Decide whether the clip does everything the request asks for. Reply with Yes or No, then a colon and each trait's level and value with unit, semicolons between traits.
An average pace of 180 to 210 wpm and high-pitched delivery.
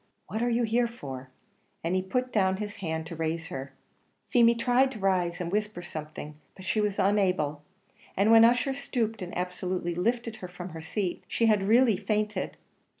Yes: average, 185 wpm; high, 195 Hz